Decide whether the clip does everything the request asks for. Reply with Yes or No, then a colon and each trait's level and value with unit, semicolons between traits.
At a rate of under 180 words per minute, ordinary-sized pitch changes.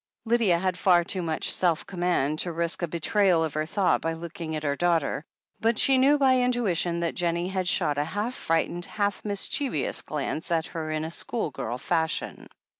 No: average, 185 wpm; average, 4.0 semitones